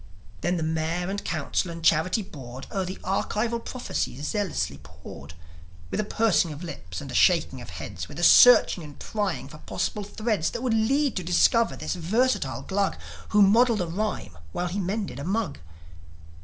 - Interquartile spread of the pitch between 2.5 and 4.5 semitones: No, average, 5.2 semitones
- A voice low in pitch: No, medium, 185 Hz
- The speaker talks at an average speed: Yes, average, 180 wpm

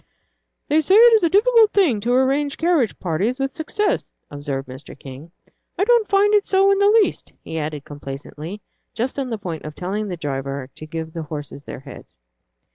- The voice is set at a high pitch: Yes, high, 210 Hz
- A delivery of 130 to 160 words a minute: No, average, 195 wpm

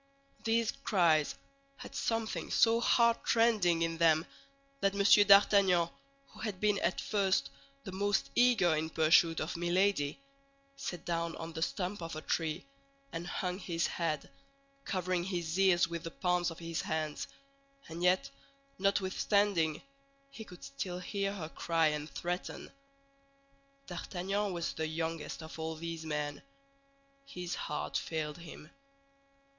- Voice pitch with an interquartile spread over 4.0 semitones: No, average, 3.4 semitones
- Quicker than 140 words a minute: No, slow, 135 wpm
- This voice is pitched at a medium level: Yes, medium, 175 Hz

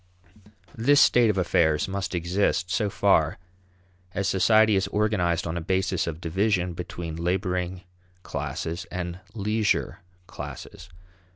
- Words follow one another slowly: Yes, slow, 120 wpm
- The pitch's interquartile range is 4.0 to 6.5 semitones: No, average, 2.8 semitones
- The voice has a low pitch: Yes, very low, 95 Hz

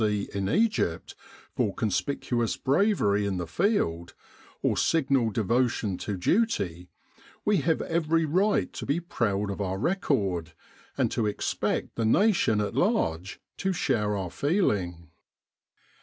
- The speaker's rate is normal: No, slow, 130 wpm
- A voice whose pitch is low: Yes, low, 110 Hz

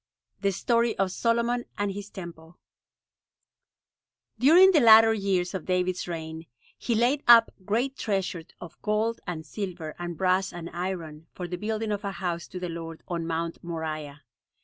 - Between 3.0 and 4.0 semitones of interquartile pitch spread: No, average, 4.6 semitones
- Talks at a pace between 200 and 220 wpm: No, average, 160 wpm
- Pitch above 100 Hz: Yes, medium, 185 Hz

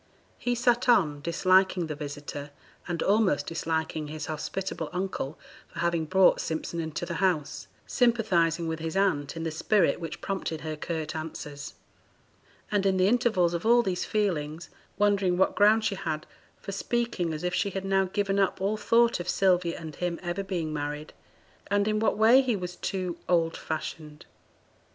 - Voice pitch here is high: No, medium, 180 Hz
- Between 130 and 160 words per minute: No, average, 170 wpm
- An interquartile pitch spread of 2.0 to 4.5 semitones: Yes, average, 3.9 semitones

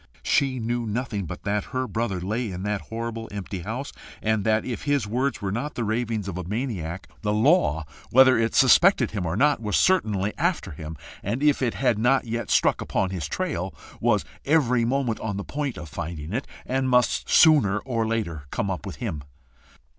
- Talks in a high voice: No, low, 115 Hz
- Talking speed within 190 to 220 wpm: Yes, average, 200 wpm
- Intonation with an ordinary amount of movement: Yes, average, 4.7 semitones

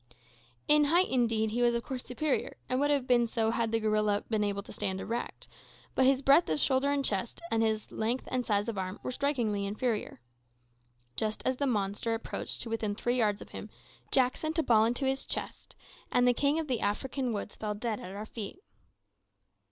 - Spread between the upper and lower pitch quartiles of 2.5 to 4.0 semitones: Yes, average, 3.7 semitones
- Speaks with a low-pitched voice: No, high, 235 Hz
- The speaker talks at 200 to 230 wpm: Yes, fast, 205 wpm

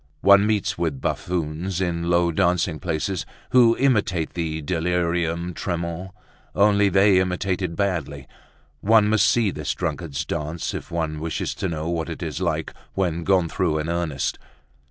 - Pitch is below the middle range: Yes, very low, 85 Hz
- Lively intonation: No, average, 3.0 semitones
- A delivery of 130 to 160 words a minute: Yes, average, 155 wpm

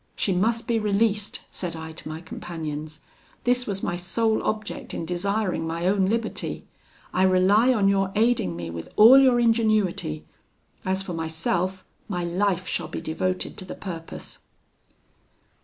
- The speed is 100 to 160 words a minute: Yes, average, 155 wpm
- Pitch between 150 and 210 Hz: Yes, high, 190 Hz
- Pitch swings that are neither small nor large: Yes, average, 4.3 semitones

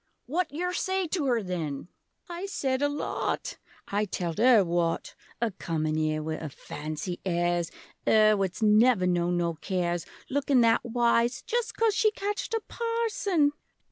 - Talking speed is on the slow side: No, average, 155 wpm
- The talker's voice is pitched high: Yes, high, 220 Hz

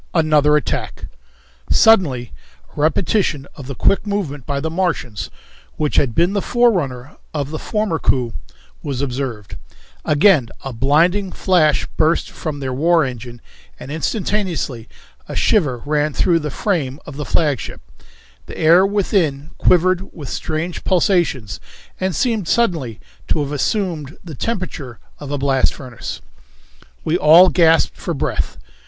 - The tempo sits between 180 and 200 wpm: No, average, 140 wpm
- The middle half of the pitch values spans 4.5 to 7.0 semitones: Yes, average, 4.9 semitones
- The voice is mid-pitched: Yes, medium, 155 Hz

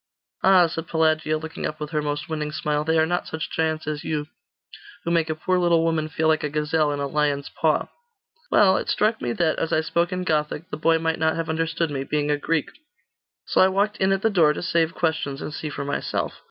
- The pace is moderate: No, fast, 235 wpm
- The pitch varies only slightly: Yes, narrow, 1.7 semitones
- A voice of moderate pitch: Yes, medium, 160 Hz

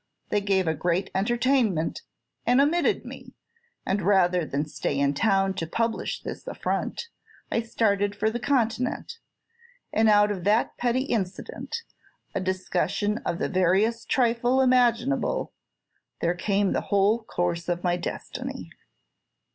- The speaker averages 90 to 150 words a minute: Yes, slow, 135 wpm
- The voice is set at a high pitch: Yes, high, 205 Hz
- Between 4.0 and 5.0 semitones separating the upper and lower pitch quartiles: Yes, average, 4.5 semitones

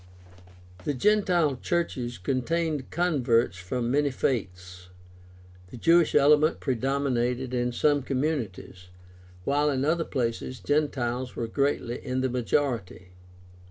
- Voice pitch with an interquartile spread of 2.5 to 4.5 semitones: Yes, average, 3.7 semitones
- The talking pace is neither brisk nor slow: No, slow, 110 wpm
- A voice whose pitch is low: Yes, low, 130 Hz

